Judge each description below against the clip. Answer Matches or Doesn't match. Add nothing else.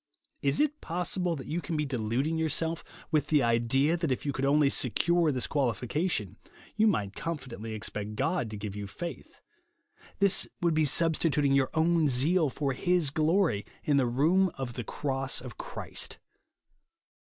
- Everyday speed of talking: Matches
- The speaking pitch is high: Doesn't match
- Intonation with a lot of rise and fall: Doesn't match